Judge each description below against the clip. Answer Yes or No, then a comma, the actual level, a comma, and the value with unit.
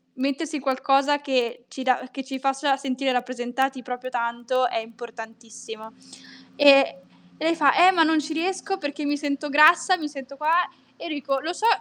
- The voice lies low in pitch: No, very high, 275 Hz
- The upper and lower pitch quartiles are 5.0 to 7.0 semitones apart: No, average, 3.1 semitones